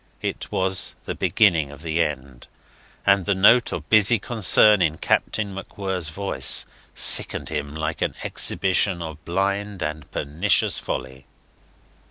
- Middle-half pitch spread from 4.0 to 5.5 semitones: Yes, average, 4.6 semitones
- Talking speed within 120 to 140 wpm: Yes, slow, 135 wpm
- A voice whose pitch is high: No, very low, 90 Hz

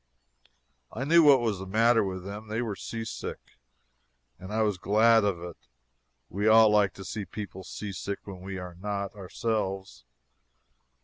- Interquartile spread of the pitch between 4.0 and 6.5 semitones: No, average, 2.7 semitones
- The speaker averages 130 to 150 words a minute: No, average, 160 wpm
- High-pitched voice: No, low, 105 Hz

